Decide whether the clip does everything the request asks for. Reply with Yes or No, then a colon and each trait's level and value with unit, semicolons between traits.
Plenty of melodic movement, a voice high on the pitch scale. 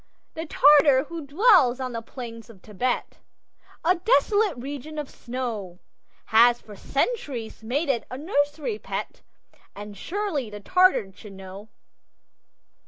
Yes: wide, 6.0 semitones; very high, 260 Hz